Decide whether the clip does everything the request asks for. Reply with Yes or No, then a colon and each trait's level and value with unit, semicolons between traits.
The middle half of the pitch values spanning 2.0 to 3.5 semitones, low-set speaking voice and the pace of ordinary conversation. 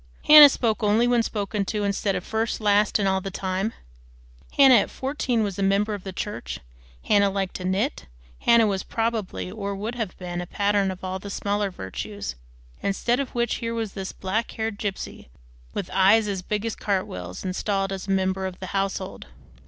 No: average, 2.7 semitones; high, 200 Hz; average, 190 wpm